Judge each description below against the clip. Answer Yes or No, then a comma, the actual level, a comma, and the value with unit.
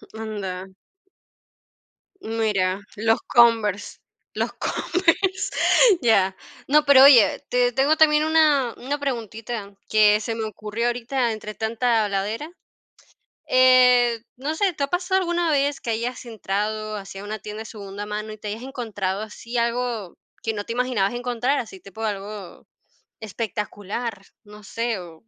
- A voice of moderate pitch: No, high, 225 Hz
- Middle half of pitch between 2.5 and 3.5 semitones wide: Yes, average, 3.2 semitones